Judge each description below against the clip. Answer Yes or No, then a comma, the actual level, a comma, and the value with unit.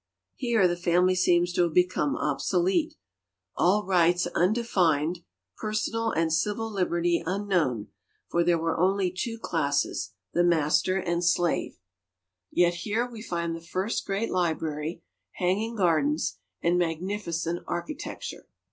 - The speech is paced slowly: Yes, slow, 125 wpm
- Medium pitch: Yes, medium, 175 Hz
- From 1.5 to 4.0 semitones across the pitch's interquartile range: Yes, average, 2.9 semitones